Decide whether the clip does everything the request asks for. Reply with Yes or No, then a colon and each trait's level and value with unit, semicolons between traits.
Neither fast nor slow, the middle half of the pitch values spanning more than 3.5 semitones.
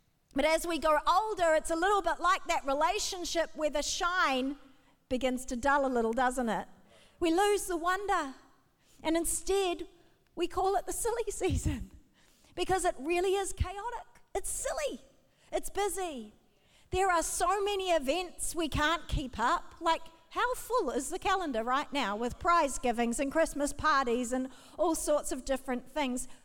Yes: average, 165 wpm; average, 4.8 semitones